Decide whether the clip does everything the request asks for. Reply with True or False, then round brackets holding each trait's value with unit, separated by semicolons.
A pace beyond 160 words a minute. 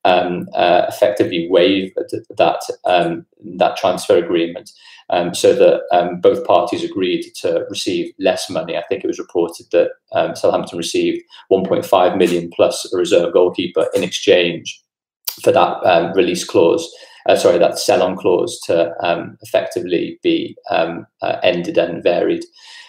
False (145 wpm)